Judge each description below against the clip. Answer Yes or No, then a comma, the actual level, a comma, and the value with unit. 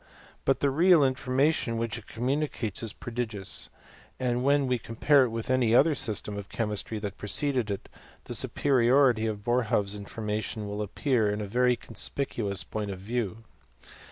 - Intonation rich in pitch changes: No, average, 3.7 semitones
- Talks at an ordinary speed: Yes, average, 160 wpm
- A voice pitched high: No, low, 115 Hz